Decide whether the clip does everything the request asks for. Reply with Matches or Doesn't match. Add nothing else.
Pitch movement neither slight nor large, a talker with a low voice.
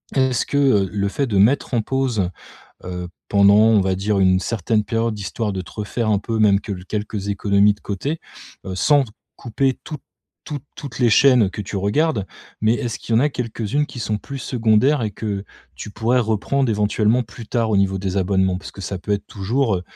Matches